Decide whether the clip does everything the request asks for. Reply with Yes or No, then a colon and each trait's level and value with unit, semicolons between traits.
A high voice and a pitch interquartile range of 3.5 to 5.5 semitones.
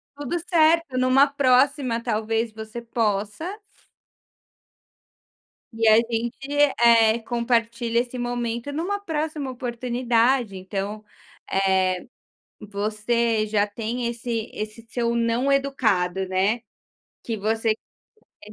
No: high, 235 Hz; average, 2.8 semitones